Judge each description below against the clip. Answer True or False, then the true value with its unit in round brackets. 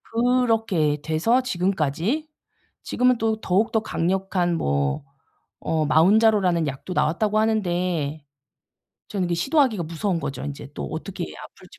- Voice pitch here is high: False (180 Hz)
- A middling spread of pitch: False (5.8 semitones)